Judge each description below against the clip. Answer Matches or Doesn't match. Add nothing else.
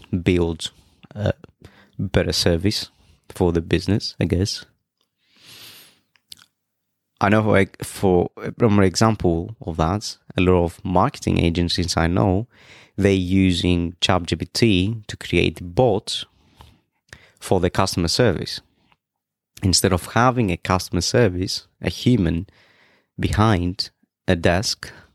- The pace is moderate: Doesn't match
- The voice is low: Matches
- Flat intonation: Doesn't match